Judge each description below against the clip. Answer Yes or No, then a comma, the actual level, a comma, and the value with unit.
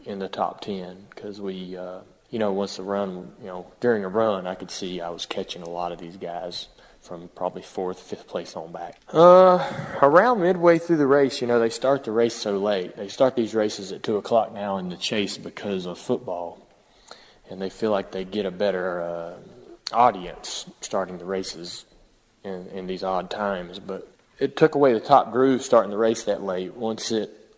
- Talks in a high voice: No, low, 100 Hz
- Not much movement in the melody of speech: No, average, 3.8 semitones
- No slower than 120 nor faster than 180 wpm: No, fast, 205 wpm